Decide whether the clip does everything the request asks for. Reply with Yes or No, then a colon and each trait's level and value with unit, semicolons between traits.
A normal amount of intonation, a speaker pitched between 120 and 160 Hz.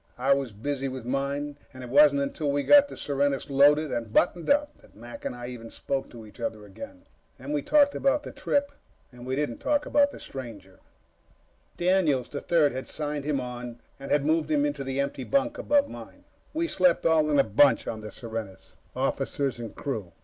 Yes: average, 4.1 semitones; medium, 140 Hz